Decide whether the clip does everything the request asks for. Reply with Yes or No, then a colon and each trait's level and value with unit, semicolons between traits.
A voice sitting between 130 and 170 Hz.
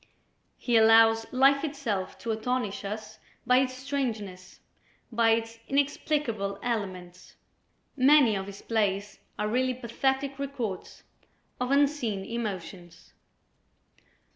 No: high, 230 Hz